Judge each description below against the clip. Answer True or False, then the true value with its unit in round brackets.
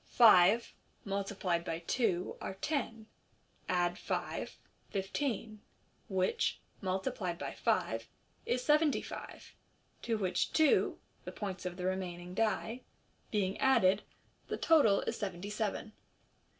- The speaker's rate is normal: False (115 wpm)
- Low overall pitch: False (195 Hz)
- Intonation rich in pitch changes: False (3.6 semitones)